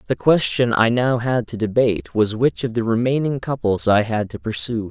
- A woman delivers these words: No, male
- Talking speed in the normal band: No, fast, 210 wpm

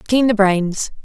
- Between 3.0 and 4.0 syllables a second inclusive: Yes, 3.3 syllables/s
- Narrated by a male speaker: No, female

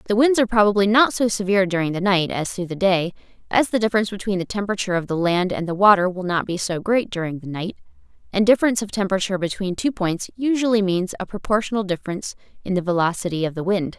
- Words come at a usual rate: No, fast, 225 wpm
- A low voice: No, high, 195 Hz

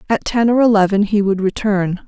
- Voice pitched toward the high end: Yes, high, 205 Hz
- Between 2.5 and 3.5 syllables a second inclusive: No, 5.3 syllables/s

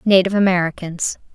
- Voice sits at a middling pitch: Yes, medium, 180 Hz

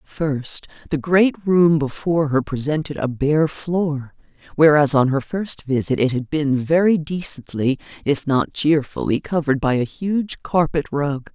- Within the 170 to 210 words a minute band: No, average, 155 wpm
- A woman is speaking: Yes, female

